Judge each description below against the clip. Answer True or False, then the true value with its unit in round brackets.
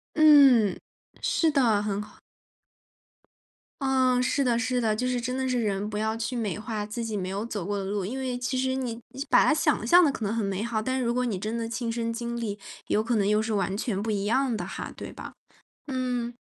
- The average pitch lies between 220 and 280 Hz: True (230 Hz)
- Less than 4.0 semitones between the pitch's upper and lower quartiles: True (3.2 semitones)